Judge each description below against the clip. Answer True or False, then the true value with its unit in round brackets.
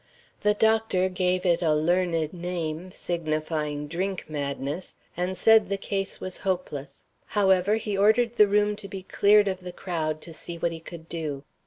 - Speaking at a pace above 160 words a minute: True (170 wpm)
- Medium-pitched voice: True (180 Hz)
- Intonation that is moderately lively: True (3.5 semitones)